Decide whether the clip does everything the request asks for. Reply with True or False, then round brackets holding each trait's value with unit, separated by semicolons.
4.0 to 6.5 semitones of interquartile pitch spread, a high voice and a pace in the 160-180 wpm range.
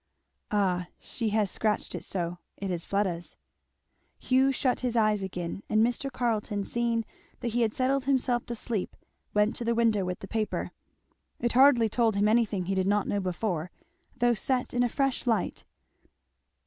False (3.5 semitones; 220 Hz; 175 wpm)